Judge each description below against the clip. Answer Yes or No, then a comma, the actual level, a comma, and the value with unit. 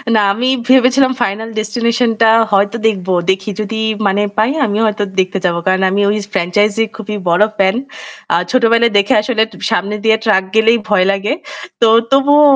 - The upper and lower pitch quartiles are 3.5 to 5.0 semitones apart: No, average, 2.8 semitones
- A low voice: No, high, 215 Hz